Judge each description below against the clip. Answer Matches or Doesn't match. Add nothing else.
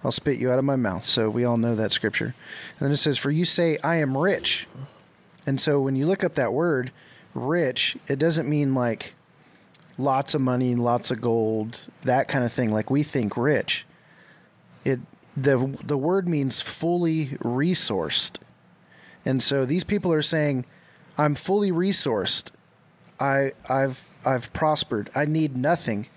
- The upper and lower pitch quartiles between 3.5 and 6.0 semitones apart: Matches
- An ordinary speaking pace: Matches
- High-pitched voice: Doesn't match